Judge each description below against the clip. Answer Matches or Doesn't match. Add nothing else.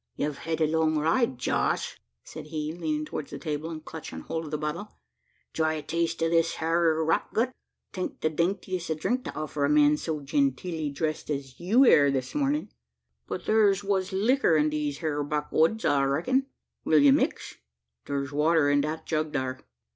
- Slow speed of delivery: Doesn't match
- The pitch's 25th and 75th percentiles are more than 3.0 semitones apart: Doesn't match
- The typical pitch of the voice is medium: Matches